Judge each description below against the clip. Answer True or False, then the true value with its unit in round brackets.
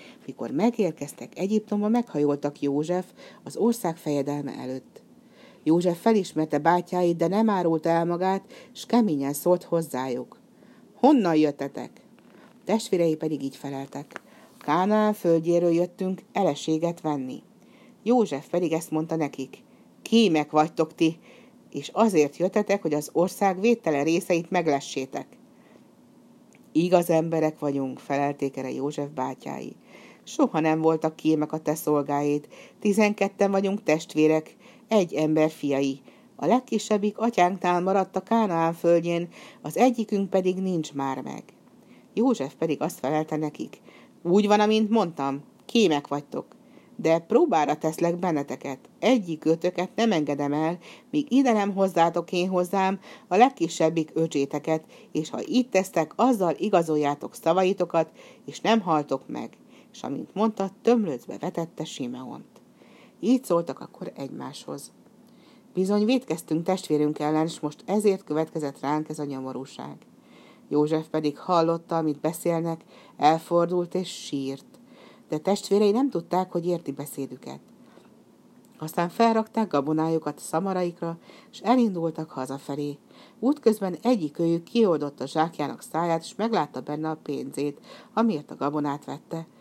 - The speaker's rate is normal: True (125 wpm)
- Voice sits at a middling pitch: True (170 Hz)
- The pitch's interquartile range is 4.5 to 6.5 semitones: True (5.4 semitones)